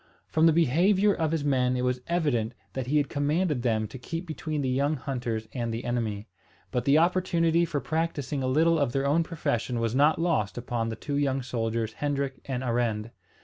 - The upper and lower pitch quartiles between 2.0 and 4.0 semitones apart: No, average, 4.8 semitones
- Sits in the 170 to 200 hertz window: No, low, 135 Hz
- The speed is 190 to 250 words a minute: Yes, average, 200 wpm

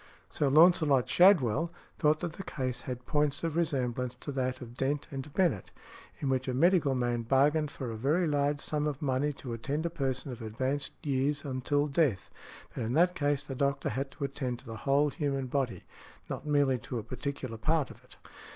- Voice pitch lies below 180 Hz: Yes, medium, 140 Hz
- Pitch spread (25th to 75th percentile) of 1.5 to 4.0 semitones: Yes, average, 2.7 semitones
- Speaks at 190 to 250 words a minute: Yes, average, 195 wpm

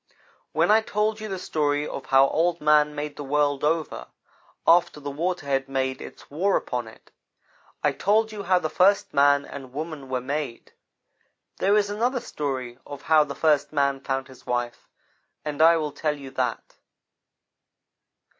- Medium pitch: Yes, medium, 150 Hz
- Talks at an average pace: Yes, average, 170 wpm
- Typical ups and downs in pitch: Yes, average, 4.2 semitones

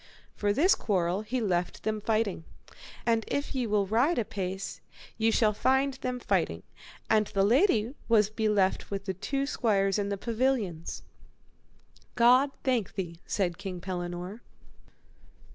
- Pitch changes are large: No, average, 3.8 semitones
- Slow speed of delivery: No, average, 145 wpm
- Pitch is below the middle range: No, high, 210 Hz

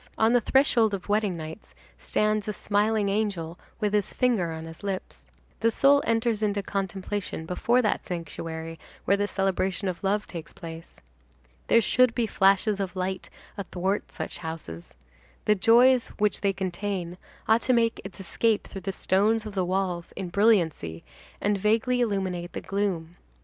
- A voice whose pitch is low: No, high, 200 Hz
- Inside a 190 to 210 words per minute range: No, average, 160 wpm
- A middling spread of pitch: Yes, average, 3.2 semitones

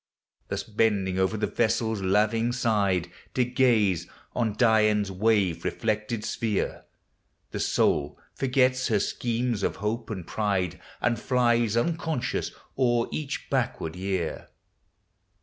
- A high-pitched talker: No, low, 110 Hz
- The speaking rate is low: Yes, slow, 115 wpm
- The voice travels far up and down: No, average, 3.4 semitones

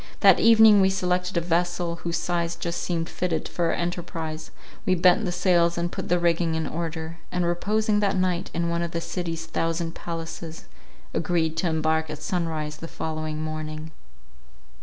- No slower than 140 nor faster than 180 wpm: Yes, average, 175 wpm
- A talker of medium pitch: Yes, medium, 170 Hz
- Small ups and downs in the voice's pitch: Yes, narrow, 1.6 semitones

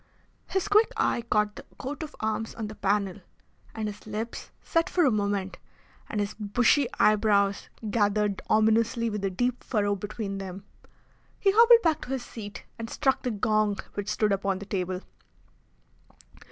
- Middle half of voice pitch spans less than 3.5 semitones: Yes, average, 3.1 semitones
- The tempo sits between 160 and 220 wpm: Yes, average, 165 wpm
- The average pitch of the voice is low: No, high, 215 Hz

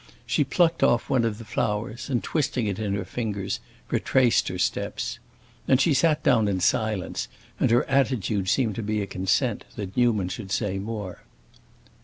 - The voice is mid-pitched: No, low, 110 Hz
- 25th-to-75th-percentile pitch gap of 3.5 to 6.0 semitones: Yes, average, 4.0 semitones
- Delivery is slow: No, average, 175 wpm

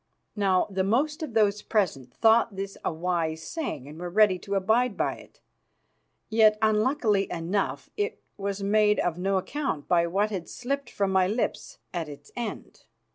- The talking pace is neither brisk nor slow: Yes, average, 170 wpm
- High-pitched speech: Yes, high, 200 Hz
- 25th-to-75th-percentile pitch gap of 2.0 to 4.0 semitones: Yes, average, 3.7 semitones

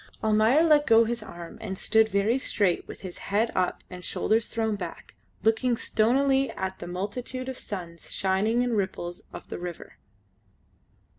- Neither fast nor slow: Yes, average, 160 wpm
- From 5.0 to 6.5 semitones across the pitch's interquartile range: No, average, 4.1 semitones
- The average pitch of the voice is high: Yes, high, 220 Hz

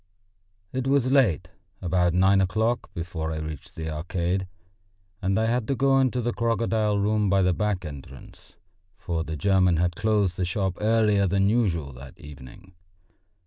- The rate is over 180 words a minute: No, average, 160 wpm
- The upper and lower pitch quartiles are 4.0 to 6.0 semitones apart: Yes, average, 4.5 semitones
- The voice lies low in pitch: Yes, very low, 95 Hz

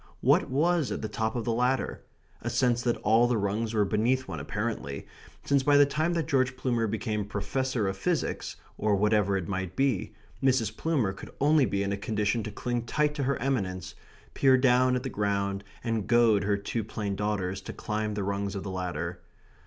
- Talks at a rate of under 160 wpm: No, average, 200 wpm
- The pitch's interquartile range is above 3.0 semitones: Yes, average, 4.3 semitones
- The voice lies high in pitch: No, low, 110 Hz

